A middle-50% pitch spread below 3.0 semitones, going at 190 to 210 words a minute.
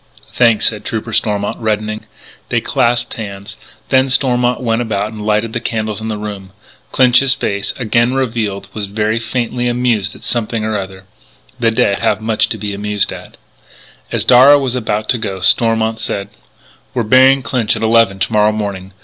No: narrow, 2.5 semitones; average, 175 wpm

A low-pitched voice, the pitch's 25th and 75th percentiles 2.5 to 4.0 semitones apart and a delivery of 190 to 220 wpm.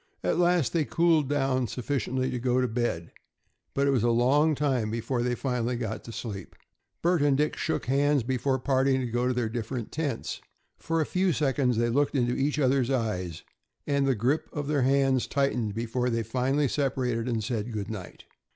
Yes: low, 130 Hz; average, 3.1 semitones; average, 195 wpm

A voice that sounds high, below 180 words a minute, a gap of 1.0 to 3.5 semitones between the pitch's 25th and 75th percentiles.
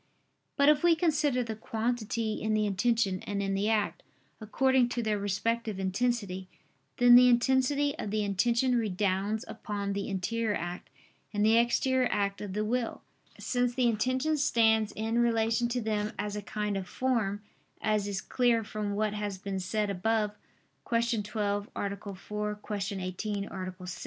Yes: high, 215 Hz; average, 165 wpm; average, 2.9 semitones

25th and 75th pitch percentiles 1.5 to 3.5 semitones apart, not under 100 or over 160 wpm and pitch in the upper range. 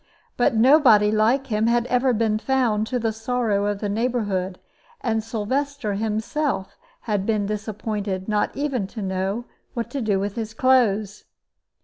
Yes: average, 3.1 semitones; average, 150 wpm; high, 220 Hz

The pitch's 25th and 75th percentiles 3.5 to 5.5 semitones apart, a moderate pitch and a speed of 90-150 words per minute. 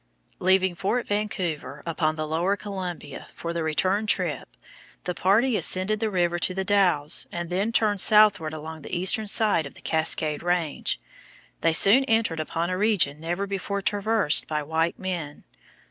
No: average, 4.0 semitones; medium, 180 Hz; average, 160 wpm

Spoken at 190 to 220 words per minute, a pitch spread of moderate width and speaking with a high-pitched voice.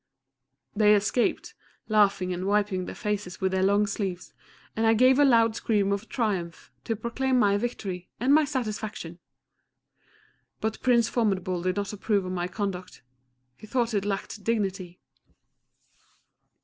No: average, 140 wpm; average, 3.1 semitones; high, 205 Hz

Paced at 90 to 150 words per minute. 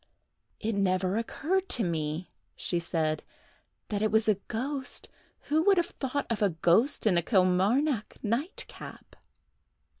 Yes: average, 140 wpm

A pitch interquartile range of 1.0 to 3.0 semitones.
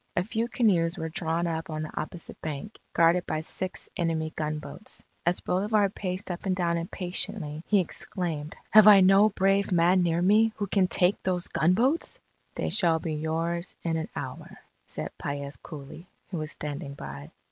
No: average, 3.5 semitones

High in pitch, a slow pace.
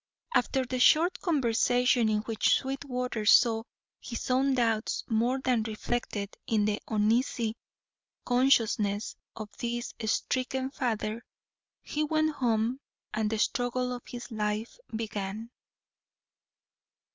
Yes: high, 235 Hz; slow, 110 wpm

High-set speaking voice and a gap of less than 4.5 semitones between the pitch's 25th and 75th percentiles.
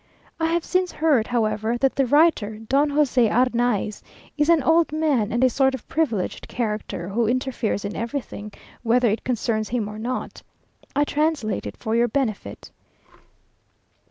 No: high, 245 Hz; average, 4.9 semitones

